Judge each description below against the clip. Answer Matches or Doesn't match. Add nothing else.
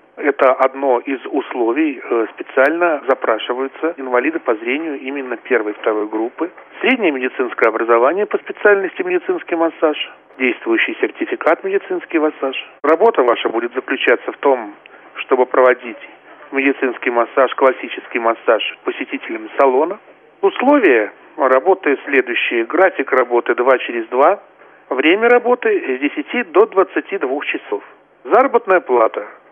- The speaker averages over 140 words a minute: Doesn't match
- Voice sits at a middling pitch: Doesn't match